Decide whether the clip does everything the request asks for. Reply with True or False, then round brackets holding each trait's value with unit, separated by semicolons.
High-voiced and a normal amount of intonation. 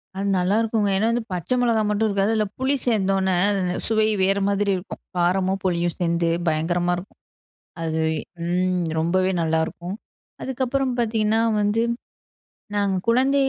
True (195 Hz; 3.9 semitones)